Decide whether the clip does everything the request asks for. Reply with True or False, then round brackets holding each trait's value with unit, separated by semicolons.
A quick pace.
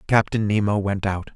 False (175 wpm)